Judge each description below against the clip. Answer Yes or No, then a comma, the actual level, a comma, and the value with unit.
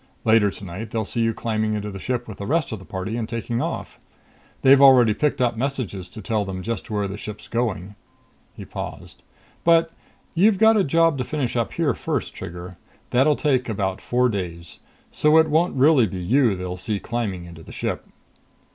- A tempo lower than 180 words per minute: No, average, 195 wpm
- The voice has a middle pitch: No, low, 115 Hz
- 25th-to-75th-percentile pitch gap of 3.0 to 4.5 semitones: No, wide, 5.5 semitones